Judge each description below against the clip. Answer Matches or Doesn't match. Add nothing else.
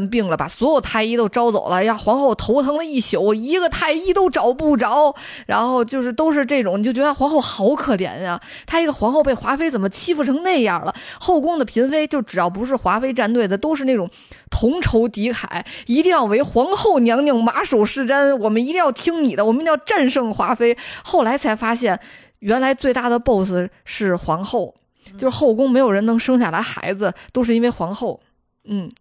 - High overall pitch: Matches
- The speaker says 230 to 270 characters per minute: Doesn't match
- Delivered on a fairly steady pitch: Doesn't match